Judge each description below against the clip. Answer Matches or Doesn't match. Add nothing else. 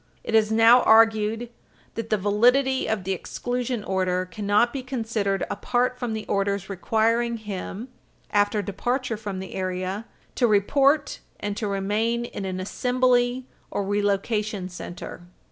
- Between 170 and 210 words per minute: Doesn't match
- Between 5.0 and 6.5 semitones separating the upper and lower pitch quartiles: Doesn't match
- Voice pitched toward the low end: Doesn't match